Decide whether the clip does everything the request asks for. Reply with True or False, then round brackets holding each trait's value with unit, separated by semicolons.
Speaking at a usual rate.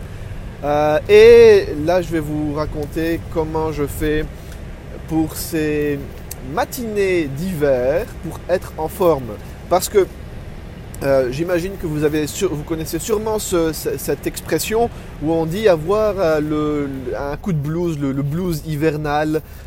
False (140 wpm)